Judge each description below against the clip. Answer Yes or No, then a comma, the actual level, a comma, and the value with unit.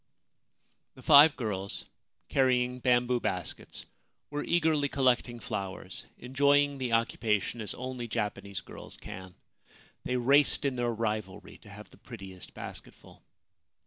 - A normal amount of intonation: Yes, average, 4.4 semitones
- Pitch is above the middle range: No, low, 120 Hz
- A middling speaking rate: No, slow, 120 wpm